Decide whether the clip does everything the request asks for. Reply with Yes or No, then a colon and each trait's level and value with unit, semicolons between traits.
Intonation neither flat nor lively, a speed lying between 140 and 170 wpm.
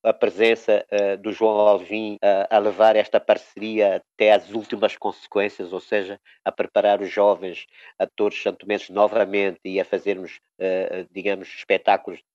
No: narrow, 1.5 semitones; average, 150 wpm